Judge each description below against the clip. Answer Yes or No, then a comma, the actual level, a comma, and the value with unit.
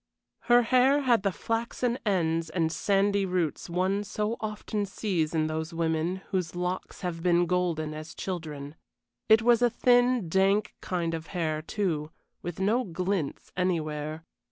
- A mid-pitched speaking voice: Yes, medium, 180 Hz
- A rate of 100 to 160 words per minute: Yes, average, 150 wpm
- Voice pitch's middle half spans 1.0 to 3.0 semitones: No, average, 4.4 semitones